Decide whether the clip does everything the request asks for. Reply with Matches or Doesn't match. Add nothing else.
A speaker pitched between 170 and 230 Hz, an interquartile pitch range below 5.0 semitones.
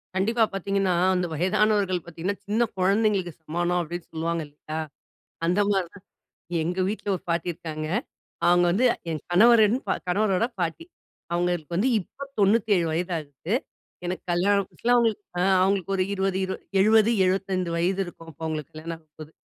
Matches